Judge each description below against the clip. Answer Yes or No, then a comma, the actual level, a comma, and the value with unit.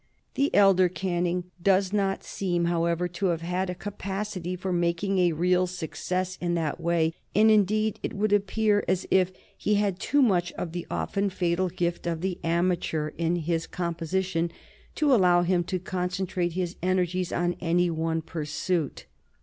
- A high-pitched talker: No, medium, 180 Hz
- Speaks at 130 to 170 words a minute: Yes, average, 165 wpm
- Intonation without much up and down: Yes, narrow, 1.9 semitones